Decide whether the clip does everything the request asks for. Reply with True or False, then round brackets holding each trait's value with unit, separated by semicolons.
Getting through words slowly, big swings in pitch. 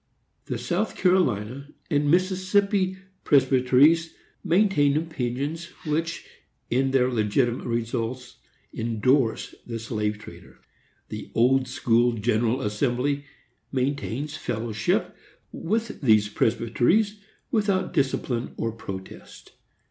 True (95 wpm; 5.8 semitones)